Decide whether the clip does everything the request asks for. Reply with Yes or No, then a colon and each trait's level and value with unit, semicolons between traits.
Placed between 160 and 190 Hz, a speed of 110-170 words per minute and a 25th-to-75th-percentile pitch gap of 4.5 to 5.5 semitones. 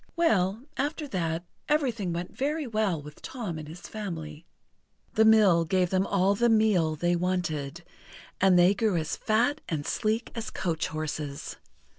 Yes: medium, 185 Hz; average, 155 wpm; average, 5.1 semitones